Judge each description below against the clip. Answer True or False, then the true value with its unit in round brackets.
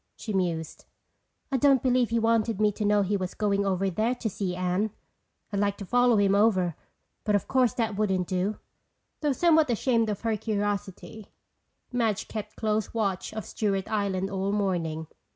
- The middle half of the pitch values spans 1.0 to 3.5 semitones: True (2.8 semitones)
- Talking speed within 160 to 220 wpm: True (175 wpm)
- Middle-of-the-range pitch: False (205 Hz)